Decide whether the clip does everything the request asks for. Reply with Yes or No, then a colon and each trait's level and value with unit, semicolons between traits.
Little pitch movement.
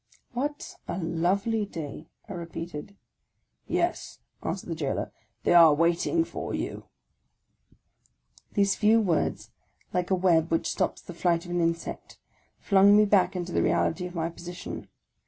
No: average, 3.2 semitones